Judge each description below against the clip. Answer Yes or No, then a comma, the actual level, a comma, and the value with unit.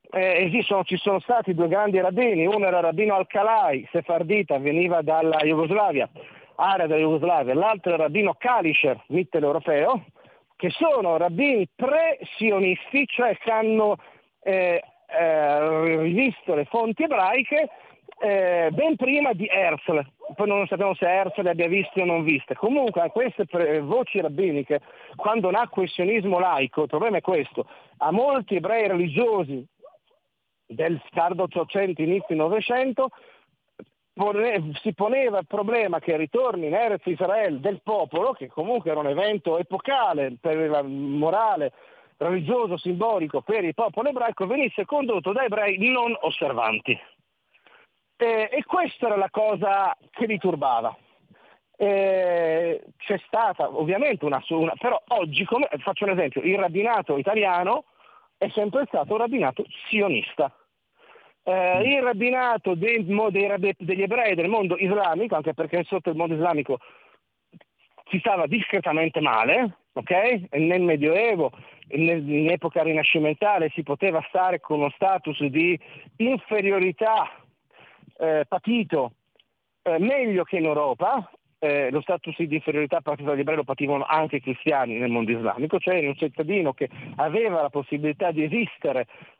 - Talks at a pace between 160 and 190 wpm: No, average, 140 wpm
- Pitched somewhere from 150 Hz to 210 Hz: Yes, medium, 185 Hz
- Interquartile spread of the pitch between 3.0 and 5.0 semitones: No, wide, 5.4 semitones